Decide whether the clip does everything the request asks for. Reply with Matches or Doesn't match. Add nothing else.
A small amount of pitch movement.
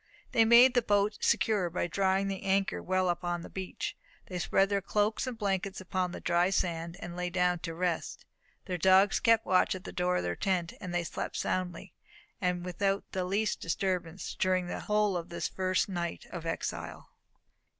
Matches